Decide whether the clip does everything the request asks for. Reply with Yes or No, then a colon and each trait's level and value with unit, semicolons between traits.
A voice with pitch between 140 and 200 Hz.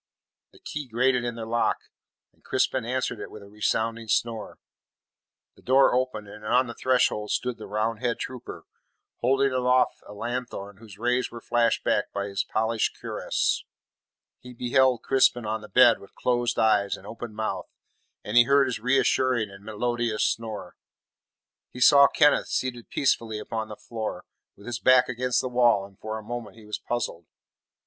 No: low, 120 Hz